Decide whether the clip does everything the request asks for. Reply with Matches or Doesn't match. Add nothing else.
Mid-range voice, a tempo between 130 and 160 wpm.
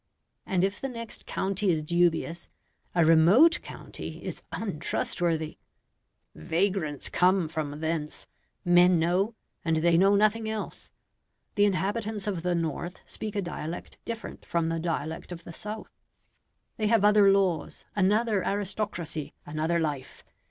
Matches